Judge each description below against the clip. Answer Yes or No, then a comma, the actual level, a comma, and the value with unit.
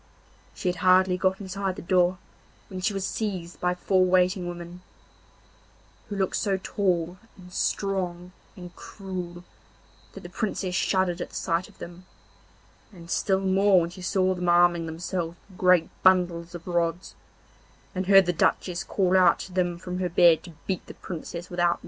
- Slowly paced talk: No, average, 175 wpm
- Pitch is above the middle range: No, medium, 180 Hz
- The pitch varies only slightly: Yes, narrow, 1.4 semitones